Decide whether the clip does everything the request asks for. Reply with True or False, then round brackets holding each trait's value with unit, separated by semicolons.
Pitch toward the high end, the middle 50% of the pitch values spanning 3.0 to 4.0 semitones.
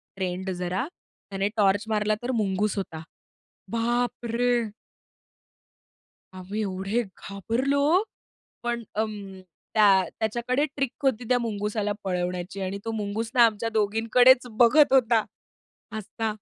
True (220 Hz; 3.5 semitones)